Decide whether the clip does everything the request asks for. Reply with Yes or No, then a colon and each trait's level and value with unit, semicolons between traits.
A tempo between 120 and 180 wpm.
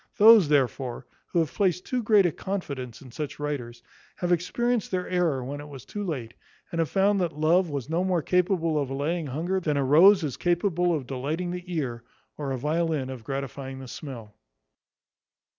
No: average, 190 wpm